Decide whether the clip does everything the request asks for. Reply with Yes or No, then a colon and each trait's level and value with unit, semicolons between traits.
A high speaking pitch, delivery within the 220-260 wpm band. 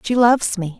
Yes: high, 215 Hz; fast, 230 wpm